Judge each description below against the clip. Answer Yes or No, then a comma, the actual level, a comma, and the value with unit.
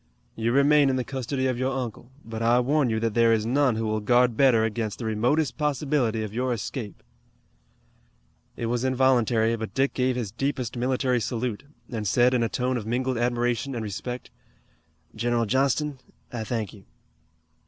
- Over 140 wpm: Yes, average, 175 wpm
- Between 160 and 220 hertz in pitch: No, low, 120 Hz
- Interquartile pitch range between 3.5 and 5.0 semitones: No, narrow, 2.6 semitones